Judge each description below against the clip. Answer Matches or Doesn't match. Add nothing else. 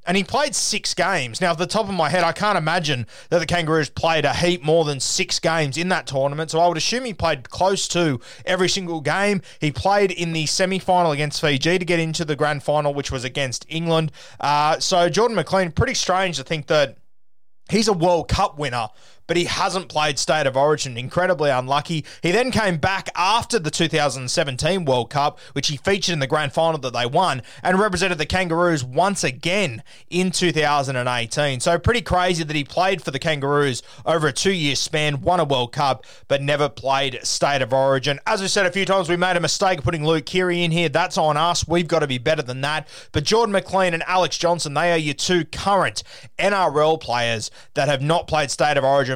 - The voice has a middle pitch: Matches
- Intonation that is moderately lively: Matches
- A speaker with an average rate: Doesn't match